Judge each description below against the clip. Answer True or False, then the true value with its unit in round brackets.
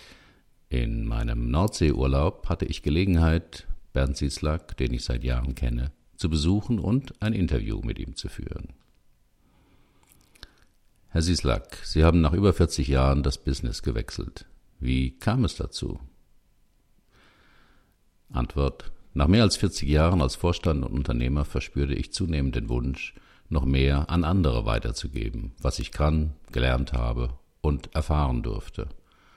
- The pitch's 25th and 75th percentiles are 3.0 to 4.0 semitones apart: False (4.9 semitones)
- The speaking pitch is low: True (75 Hz)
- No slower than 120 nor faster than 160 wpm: True (135 wpm)